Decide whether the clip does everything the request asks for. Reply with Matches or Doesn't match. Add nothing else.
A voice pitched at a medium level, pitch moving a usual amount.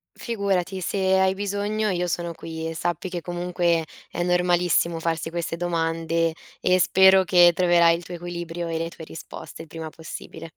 Doesn't match